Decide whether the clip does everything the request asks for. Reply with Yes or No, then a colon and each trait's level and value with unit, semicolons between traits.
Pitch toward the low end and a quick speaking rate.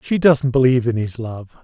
Yes: low, 125 Hz; fast, 220 wpm